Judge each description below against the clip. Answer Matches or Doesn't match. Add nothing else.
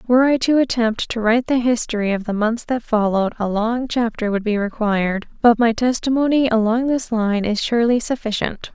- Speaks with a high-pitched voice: Matches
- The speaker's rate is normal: Matches